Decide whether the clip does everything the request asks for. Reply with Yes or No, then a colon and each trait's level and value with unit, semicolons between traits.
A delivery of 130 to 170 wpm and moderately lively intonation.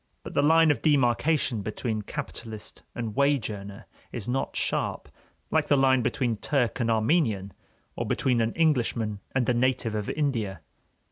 Yes: average, 155 wpm; average, 4.4 semitones